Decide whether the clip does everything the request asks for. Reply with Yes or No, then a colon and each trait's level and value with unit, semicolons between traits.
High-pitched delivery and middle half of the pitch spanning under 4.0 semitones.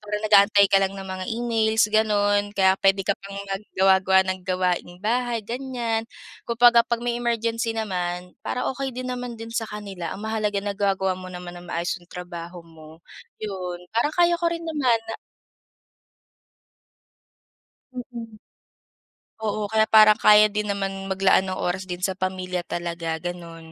Yes: high, 200 Hz; average, 3.6 semitones